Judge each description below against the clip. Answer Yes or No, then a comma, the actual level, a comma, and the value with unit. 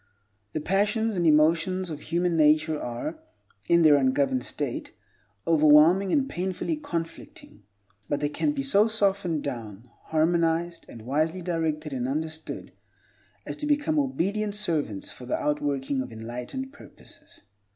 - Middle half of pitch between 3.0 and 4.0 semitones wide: No, average, 5.1 semitones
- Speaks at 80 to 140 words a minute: Yes, slow, 135 wpm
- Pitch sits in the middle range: Yes, medium, 160 Hz